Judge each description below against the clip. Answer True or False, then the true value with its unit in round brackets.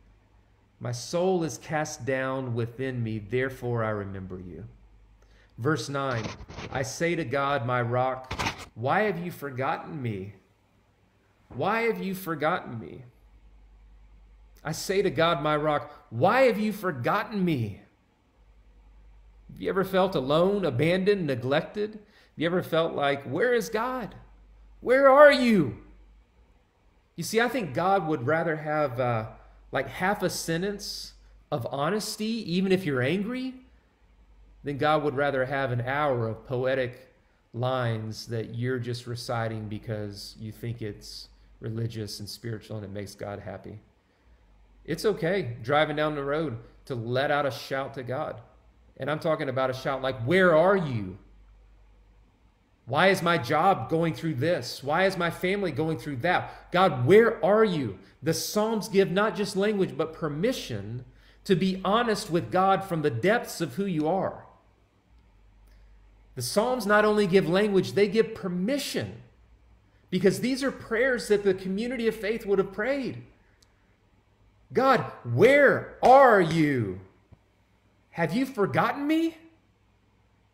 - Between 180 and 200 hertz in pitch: False (140 Hz)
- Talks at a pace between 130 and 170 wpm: True (145 wpm)